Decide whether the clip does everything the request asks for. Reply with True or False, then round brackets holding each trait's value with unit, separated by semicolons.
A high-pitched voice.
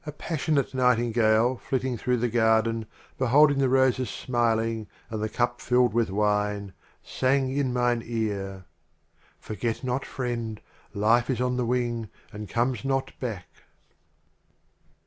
False (120 Hz)